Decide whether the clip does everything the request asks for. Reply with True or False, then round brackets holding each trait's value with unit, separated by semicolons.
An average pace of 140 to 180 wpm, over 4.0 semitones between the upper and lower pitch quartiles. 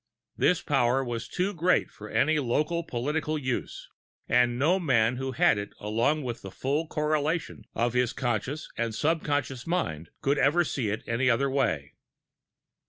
True (160 wpm; 4.5 semitones)